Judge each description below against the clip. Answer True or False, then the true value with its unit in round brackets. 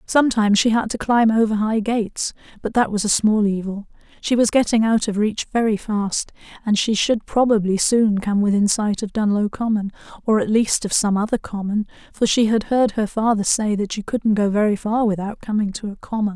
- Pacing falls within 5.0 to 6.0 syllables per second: True (5.3 syllables/s)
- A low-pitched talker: False (215 Hz)